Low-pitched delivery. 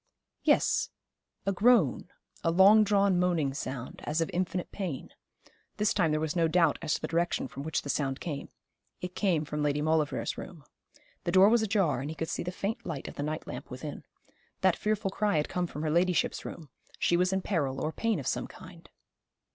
No: medium, 170 Hz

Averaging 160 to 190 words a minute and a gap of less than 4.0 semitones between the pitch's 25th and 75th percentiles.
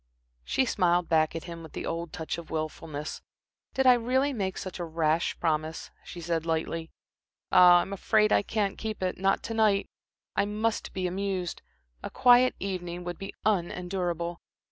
Yes: average, 170 wpm; average, 3.6 semitones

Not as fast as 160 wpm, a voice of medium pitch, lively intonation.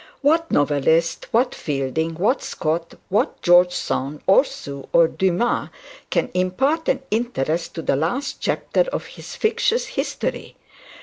Yes: slow, 135 wpm; medium, 180 Hz; wide, 8.0 semitones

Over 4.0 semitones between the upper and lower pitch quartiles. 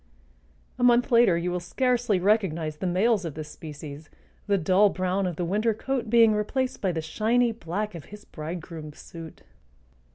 Yes: average, 5.2 semitones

